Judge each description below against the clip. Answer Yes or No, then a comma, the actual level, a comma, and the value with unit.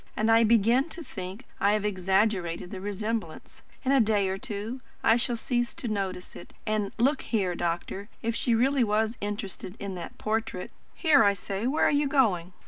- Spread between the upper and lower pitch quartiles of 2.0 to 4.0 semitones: Yes, average, 3.5 semitones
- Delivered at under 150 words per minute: No, average, 190 wpm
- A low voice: No, high, 215 Hz